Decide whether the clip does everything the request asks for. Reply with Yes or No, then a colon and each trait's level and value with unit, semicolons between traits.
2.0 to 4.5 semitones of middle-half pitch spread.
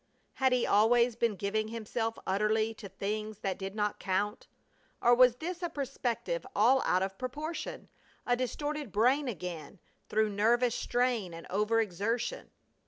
Yes: average, 3.5 semitones